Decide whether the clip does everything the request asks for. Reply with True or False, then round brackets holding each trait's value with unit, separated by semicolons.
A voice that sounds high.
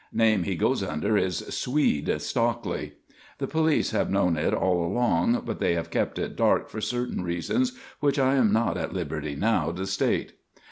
False (105 Hz)